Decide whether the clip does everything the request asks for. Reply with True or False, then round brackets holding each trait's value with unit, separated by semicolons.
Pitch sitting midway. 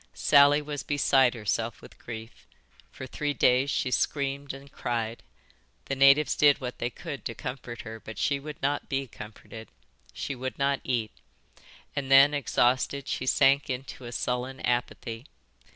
False (130 Hz)